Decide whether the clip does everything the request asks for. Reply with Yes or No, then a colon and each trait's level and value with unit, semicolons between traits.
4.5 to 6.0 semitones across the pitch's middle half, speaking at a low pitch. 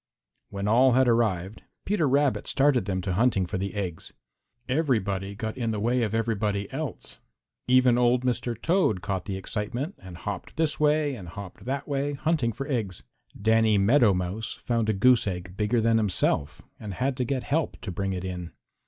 Yes: average, 4.8 semitones; low, 115 Hz